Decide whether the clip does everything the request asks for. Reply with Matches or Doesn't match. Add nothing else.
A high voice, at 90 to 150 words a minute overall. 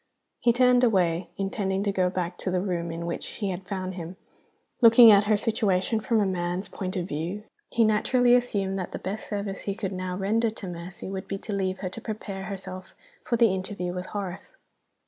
Doesn't match